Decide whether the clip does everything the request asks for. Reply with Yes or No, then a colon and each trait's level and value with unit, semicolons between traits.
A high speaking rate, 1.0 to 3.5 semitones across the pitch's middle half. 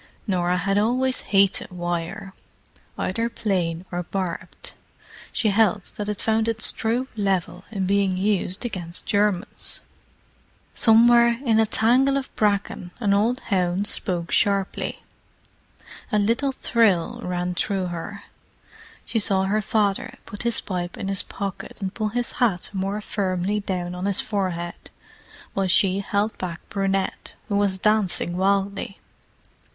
No: slow, 135 wpm; average, 2.9 semitones